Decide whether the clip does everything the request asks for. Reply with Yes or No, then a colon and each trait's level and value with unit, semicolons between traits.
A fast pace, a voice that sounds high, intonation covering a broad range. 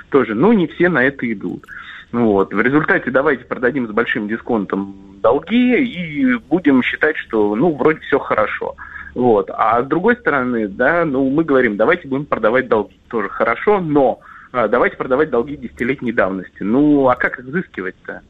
No: fast, 165 wpm; low, 135 Hz; wide, 6.9 semitones